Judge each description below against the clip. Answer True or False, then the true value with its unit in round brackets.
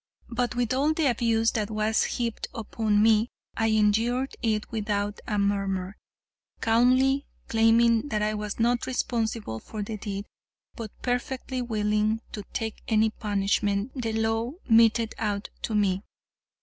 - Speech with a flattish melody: True (2.1 semitones)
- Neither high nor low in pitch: False (220 Hz)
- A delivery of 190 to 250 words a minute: False (140 wpm)